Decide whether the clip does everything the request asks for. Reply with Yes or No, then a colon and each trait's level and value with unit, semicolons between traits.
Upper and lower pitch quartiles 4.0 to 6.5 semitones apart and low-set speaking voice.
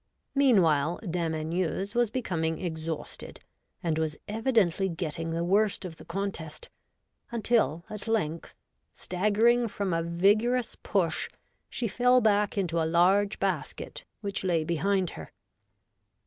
No: average, 4.4 semitones; medium, 185 Hz